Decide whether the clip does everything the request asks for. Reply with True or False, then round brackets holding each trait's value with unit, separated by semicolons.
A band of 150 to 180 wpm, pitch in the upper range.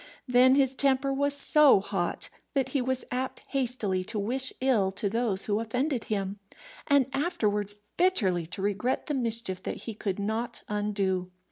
True (160 wpm; 230 Hz)